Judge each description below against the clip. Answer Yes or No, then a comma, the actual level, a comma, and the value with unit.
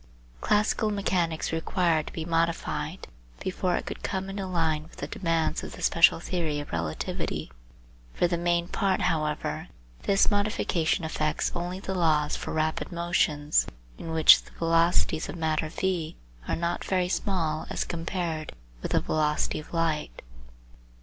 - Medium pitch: Yes, medium, 165 Hz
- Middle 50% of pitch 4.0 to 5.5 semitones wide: No, narrow, 2.4 semitones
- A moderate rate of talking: Yes, average, 150 wpm